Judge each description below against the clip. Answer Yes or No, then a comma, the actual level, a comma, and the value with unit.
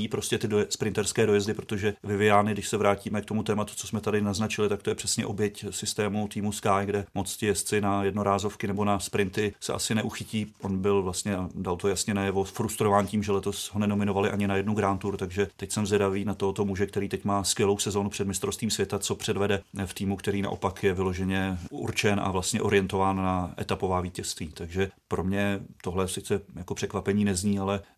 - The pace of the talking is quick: Yes, fast, 200 wpm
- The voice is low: Yes, low, 100 Hz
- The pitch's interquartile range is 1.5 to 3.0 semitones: No, narrow, 1.1 semitones